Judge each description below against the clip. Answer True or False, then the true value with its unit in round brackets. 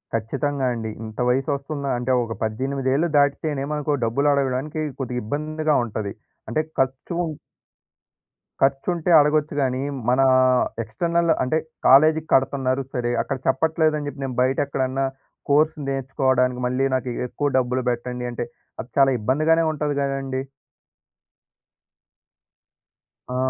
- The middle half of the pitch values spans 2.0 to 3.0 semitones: True (2.7 semitones)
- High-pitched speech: False (135 Hz)